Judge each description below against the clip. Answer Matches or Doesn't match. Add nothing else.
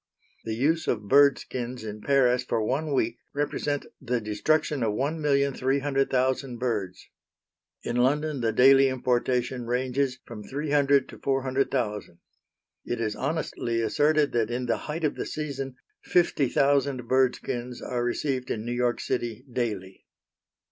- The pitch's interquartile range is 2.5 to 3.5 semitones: Matches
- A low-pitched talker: Matches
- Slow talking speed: Doesn't match